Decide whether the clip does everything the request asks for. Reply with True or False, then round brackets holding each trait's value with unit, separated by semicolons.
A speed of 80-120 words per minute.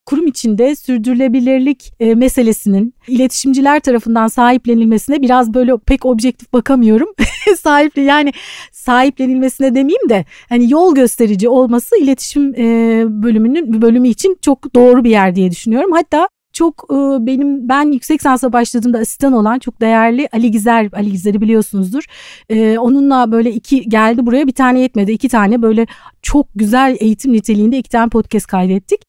False (135 wpm)